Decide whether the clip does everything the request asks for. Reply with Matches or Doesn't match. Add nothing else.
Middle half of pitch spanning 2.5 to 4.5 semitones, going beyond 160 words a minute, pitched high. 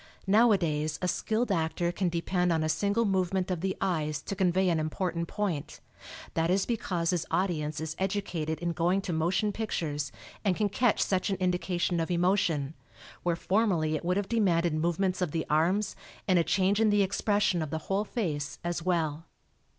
Doesn't match